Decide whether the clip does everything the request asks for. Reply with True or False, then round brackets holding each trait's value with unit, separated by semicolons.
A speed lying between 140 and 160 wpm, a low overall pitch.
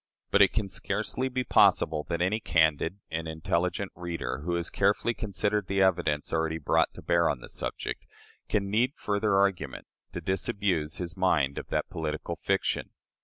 False (170 wpm; 90 Hz)